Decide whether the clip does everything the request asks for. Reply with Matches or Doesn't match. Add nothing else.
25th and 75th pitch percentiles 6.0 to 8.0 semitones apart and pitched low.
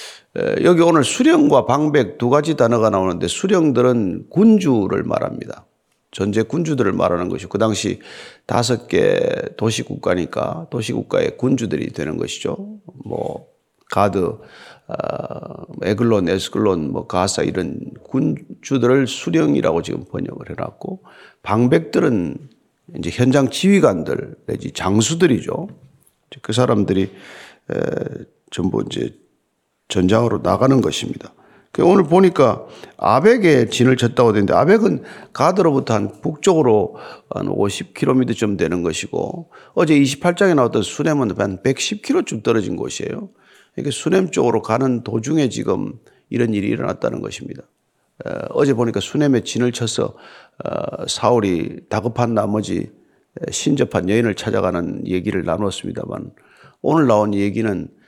Matches